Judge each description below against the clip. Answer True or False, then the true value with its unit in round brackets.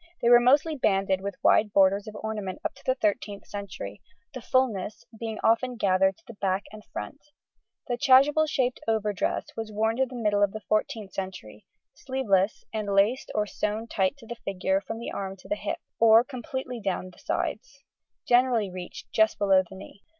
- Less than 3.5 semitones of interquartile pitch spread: False (3.8 semitones)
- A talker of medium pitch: False (215 Hz)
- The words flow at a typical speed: True (185 wpm)